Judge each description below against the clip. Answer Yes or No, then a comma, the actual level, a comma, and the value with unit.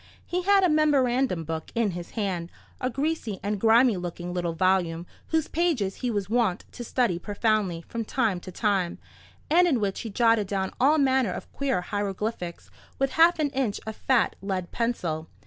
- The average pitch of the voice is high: Yes, high, 215 Hz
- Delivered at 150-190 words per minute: Yes, average, 175 wpm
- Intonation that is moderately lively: No, wide, 6.0 semitones